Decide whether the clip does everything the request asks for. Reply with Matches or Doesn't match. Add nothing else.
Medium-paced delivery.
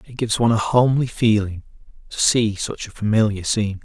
Matches